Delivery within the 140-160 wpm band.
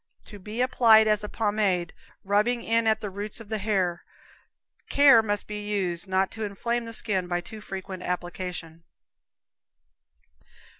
Yes: average, 150 wpm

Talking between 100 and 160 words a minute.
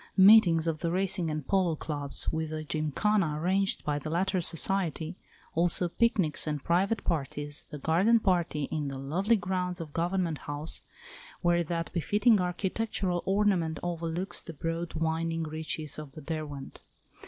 Yes: average, 150 wpm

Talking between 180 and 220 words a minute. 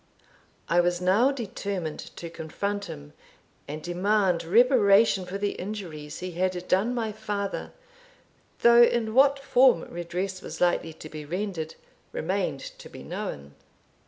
No: slow, 135 wpm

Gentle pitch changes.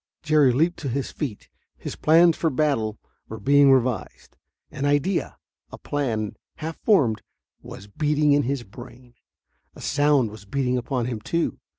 No: average, 4.0 semitones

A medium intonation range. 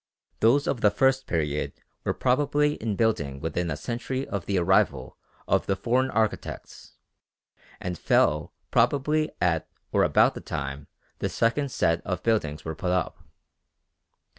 No: wide, 7.7 semitones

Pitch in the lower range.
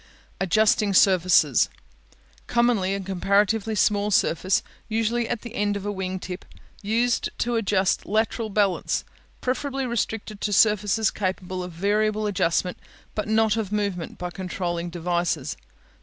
No: high, 205 Hz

